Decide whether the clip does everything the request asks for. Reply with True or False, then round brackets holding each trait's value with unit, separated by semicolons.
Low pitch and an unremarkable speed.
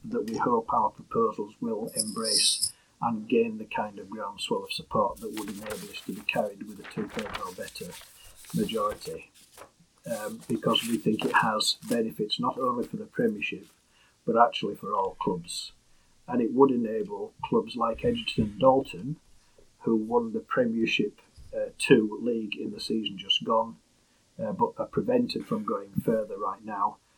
False (230 Hz; 165 wpm)